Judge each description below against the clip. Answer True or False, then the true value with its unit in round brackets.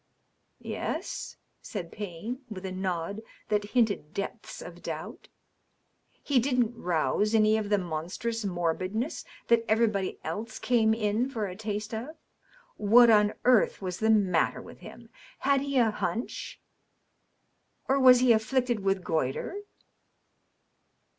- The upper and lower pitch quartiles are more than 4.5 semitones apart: False (3.5 semitones)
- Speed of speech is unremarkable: False (130 wpm)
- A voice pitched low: False (215 Hz)